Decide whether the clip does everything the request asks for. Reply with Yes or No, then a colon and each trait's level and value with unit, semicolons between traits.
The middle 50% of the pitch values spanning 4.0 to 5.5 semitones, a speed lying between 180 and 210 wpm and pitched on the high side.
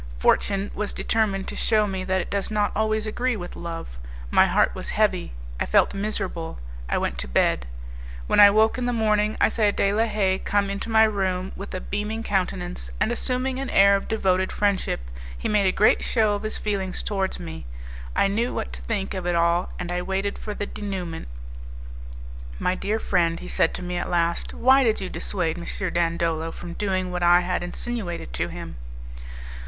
No: average, 3.2 semitones; average, 200 wpm; high, 195 Hz